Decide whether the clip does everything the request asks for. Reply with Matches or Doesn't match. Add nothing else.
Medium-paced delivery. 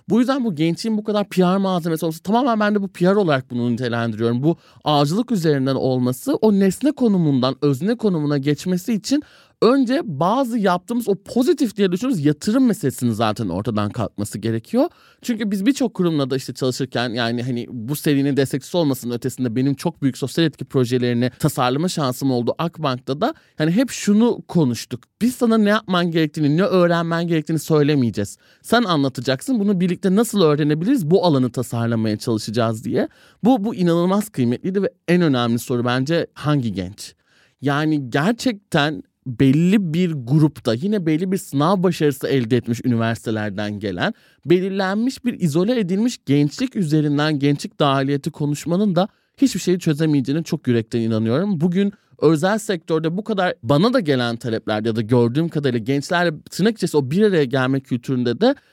Doesn't match